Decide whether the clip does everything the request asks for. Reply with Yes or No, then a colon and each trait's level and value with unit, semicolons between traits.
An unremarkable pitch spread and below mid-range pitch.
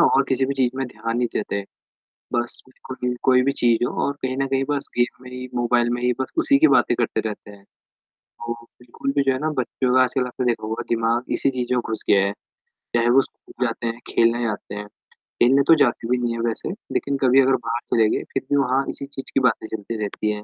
No: narrow, 2.3 semitones; low, 125 Hz